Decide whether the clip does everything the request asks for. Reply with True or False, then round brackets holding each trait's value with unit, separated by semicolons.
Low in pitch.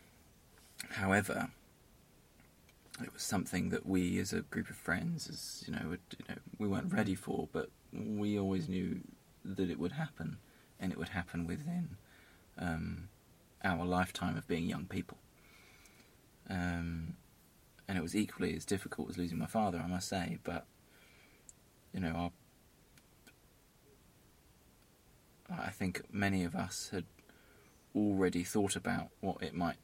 True (90 Hz)